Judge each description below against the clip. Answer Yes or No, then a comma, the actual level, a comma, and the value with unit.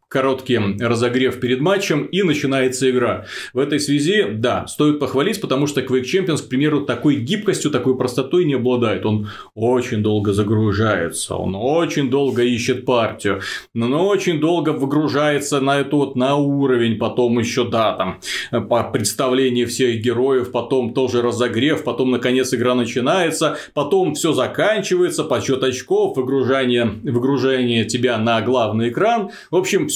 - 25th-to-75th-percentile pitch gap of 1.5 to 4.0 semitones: Yes, average, 3.3 semitones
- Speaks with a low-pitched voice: Yes, low, 130 Hz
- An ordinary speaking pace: Yes, average, 140 wpm